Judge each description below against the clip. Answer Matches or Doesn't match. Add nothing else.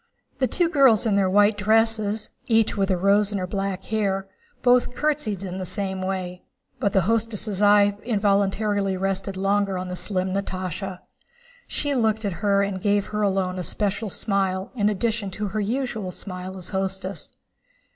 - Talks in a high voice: Matches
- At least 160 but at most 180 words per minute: Matches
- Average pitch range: Doesn't match